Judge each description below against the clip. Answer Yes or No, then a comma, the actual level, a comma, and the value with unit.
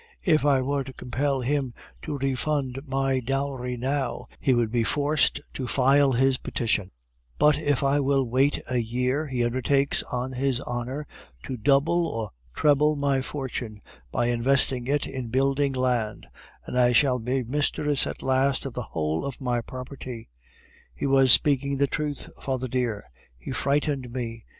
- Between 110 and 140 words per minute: No, average, 160 wpm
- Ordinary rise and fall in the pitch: No, narrow, 2.3 semitones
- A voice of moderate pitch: No, low, 130 Hz